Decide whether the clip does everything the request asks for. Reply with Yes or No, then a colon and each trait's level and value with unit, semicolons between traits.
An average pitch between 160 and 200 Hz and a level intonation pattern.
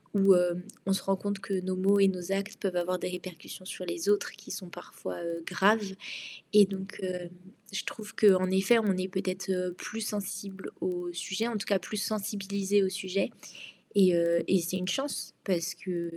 Yes: high, 190 Hz; narrow, 1.8 semitones